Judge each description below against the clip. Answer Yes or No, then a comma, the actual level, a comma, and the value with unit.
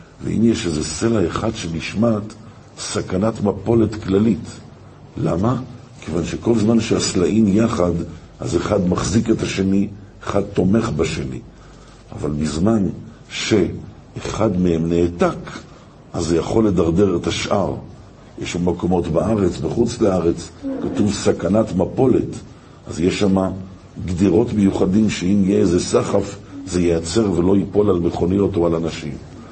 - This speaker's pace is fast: No, average, 125 wpm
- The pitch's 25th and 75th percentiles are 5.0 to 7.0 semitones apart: No, average, 3.7 semitones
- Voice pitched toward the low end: Yes, very low, 95 Hz